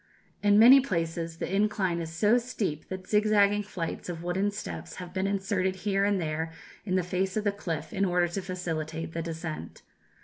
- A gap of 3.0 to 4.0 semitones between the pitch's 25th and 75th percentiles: Yes, average, 3.4 semitones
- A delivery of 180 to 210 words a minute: Yes, average, 190 wpm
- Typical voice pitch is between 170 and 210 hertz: Yes, medium, 185 Hz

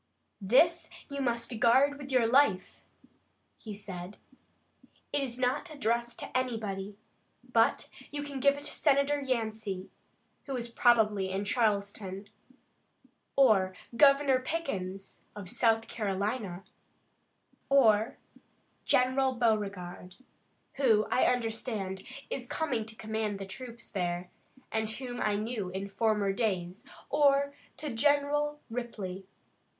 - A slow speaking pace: Yes, slow, 115 wpm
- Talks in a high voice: Yes, high, 225 Hz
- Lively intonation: No, average, 4.8 semitones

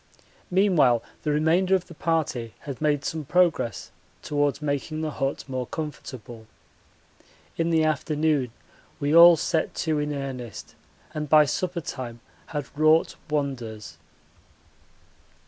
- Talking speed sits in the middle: No, slow, 125 wpm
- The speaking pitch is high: No, medium, 150 Hz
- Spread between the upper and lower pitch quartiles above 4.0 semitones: No, average, 2.9 semitones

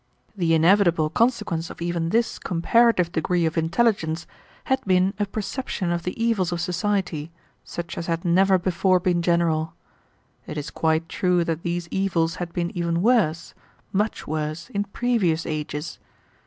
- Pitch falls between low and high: Yes, medium, 175 Hz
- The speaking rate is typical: Yes, average, 155 wpm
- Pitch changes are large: No, average, 2.9 semitones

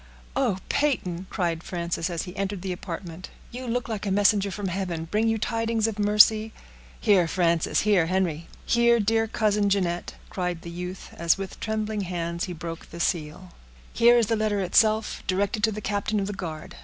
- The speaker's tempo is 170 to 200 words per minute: Yes, average, 180 wpm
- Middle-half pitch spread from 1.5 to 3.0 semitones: No, average, 3.8 semitones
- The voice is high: Yes, high, 195 Hz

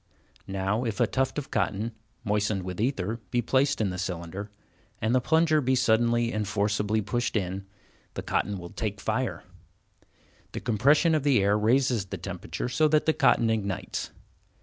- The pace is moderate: Yes, average, 170 wpm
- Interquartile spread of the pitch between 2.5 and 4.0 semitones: No, average, 4.5 semitones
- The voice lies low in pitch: Yes, low, 110 Hz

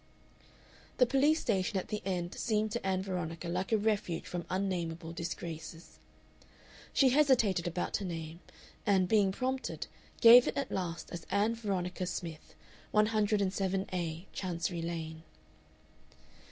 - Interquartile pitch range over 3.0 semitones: Yes, average, 3.8 semitones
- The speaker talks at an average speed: No, slow, 125 wpm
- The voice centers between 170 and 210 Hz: Yes, high, 190 Hz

